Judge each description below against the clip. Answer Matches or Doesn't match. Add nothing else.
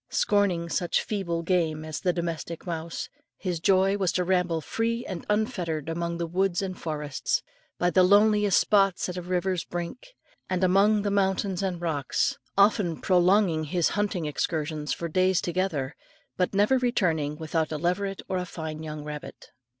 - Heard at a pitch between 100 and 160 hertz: Doesn't match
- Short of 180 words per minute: Matches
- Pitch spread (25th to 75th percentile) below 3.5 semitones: Matches